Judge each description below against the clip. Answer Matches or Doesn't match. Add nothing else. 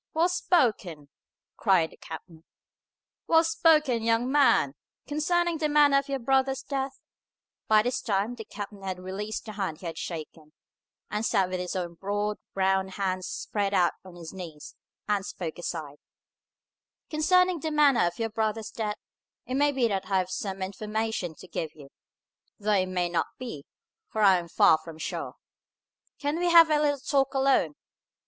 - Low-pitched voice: Doesn't match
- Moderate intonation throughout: Doesn't match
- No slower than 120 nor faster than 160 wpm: Doesn't match